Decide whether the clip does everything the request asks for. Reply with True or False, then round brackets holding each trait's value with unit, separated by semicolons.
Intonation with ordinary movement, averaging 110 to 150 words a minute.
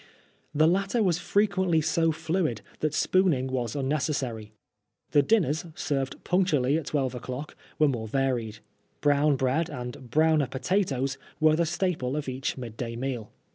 True (4.2 semitones; 145 wpm)